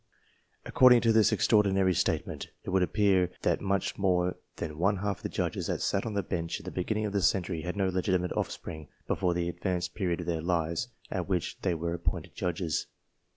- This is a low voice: Yes, very low, 90 Hz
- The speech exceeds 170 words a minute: Yes, average, 200 wpm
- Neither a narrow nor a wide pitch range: No, narrow, 2.3 semitones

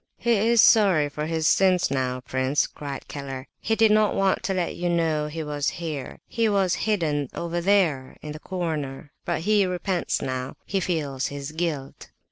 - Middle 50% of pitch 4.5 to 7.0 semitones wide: Yes, average, 5.0 semitones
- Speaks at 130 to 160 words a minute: No, average, 175 wpm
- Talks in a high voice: No, medium, 160 Hz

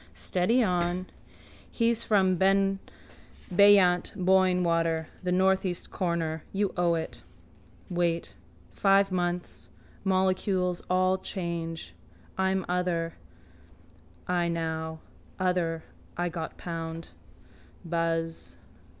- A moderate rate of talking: No, slow, 90 wpm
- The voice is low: No, medium, 180 Hz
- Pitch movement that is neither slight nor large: No, narrow, 2.2 semitones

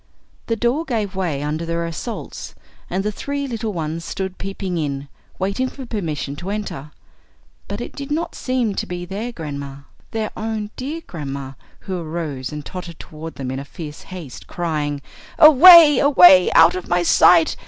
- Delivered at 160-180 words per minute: Yes, average, 165 wpm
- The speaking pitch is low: No, medium, 180 Hz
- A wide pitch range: Yes, wide, 6.5 semitones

